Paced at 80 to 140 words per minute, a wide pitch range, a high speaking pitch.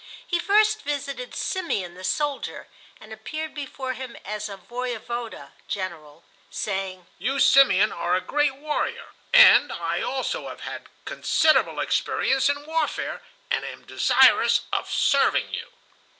Yes: slow, 135 wpm; wide, 7.0 semitones; very high, 255 Hz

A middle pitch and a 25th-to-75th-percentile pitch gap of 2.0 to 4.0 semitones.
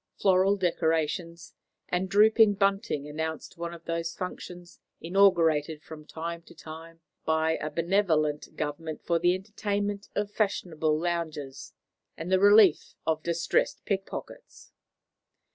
Yes: medium, 170 Hz; average, 3.3 semitones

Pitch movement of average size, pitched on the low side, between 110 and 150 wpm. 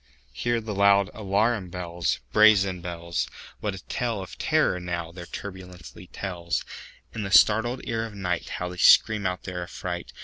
Yes: average, 3.2 semitones; very low, 95 Hz; average, 140 wpm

